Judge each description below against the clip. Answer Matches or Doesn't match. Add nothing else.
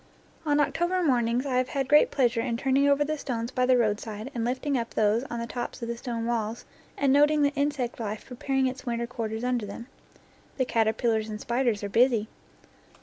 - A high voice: Matches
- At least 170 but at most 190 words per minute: Doesn't match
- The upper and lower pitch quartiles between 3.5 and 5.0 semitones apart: Doesn't match